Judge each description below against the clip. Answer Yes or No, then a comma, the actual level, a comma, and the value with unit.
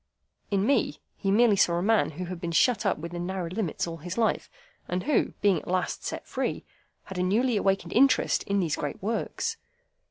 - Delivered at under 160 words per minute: No, average, 200 wpm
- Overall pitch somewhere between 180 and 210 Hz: Yes, high, 190 Hz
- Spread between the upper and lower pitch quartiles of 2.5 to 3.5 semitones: No, average, 4.0 semitones